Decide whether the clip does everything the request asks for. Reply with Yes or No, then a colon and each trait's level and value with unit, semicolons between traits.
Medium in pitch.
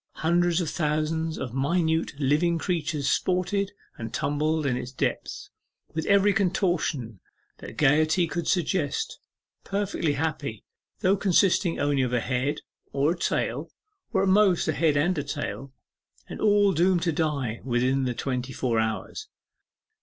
Yes: medium, 155 Hz